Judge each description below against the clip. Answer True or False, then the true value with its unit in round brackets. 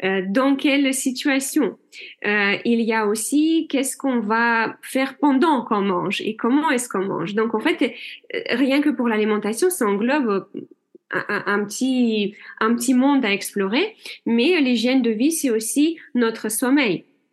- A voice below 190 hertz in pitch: False (250 Hz)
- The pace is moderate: True (155 wpm)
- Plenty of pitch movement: False (4.9 semitones)